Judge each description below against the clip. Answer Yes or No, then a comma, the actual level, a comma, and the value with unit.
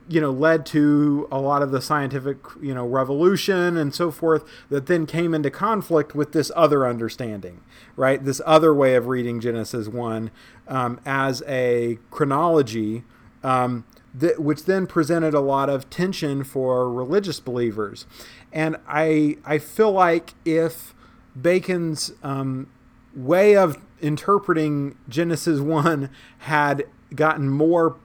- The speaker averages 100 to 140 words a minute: Yes, slow, 135 wpm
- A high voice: No, medium, 145 Hz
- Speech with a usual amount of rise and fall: Yes, average, 4.1 semitones